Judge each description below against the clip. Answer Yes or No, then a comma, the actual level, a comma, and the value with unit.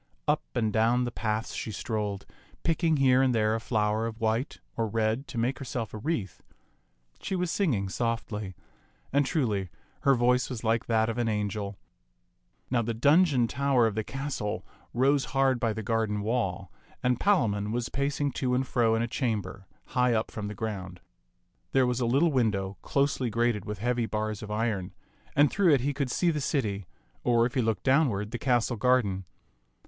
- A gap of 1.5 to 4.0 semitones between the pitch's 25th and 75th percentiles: Yes, average, 3.6 semitones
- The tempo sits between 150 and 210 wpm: Yes, average, 185 wpm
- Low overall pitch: Yes, low, 115 Hz